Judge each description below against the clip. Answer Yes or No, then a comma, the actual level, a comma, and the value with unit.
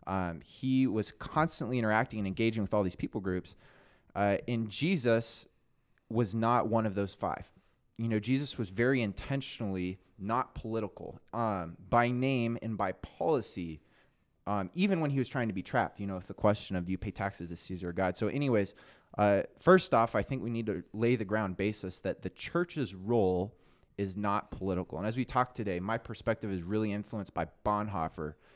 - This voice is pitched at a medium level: No, low, 105 Hz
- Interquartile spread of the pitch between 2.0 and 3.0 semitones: No, average, 3.9 semitones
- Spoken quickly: No, average, 190 wpm